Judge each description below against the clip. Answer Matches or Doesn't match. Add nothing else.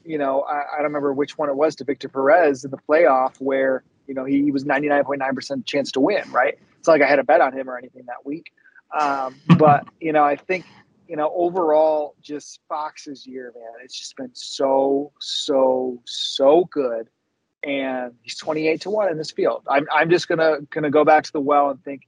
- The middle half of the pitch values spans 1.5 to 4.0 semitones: Matches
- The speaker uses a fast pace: Matches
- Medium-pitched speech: Matches